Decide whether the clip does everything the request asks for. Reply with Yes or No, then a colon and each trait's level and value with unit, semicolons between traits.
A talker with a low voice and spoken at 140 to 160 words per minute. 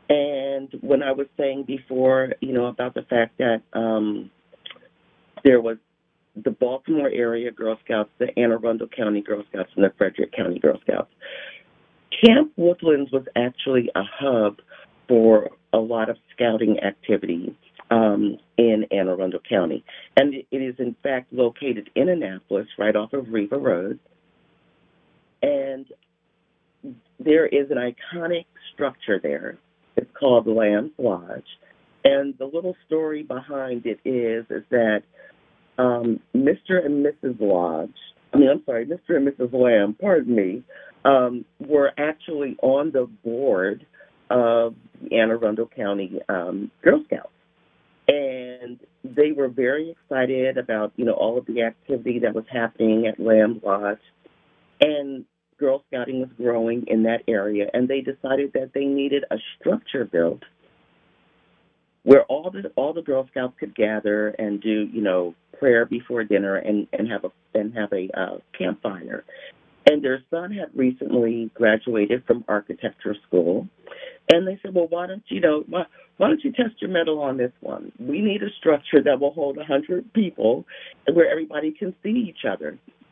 Yes: low, 130 Hz; average, 155 wpm